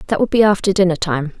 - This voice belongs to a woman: Yes, female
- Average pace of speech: No, fast, 255 wpm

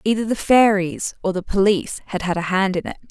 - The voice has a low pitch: No, high, 200 Hz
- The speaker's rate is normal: No, fast, 230 wpm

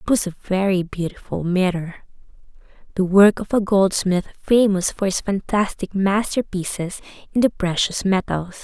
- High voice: Yes, high, 195 Hz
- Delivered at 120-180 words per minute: Yes, average, 140 wpm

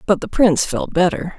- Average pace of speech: No, fast, 215 wpm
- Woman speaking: Yes, female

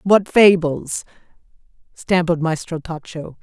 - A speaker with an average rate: No, slow, 90 wpm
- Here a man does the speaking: No, female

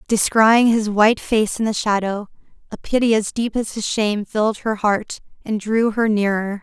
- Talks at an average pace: Yes, average, 190 wpm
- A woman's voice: Yes, female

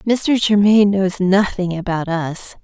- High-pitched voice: Yes, high, 195 Hz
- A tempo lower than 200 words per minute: Yes, slow, 135 wpm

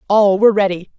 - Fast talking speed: No, average, 185 wpm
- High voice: Yes, high, 200 Hz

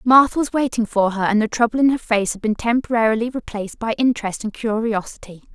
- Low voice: No, high, 225 Hz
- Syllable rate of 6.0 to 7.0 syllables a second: Yes, 6.2 syllables/s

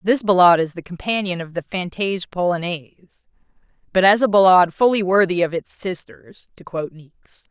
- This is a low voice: No, medium, 180 Hz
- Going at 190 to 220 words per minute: No, average, 170 wpm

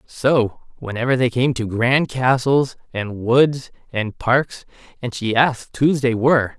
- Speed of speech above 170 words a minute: No, average, 155 wpm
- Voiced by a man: Yes, male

